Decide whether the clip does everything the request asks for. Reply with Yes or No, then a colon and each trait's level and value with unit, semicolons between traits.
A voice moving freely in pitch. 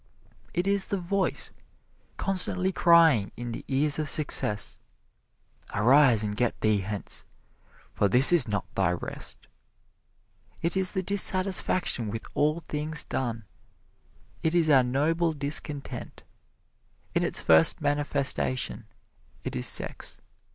Yes: wide, 6.8 semitones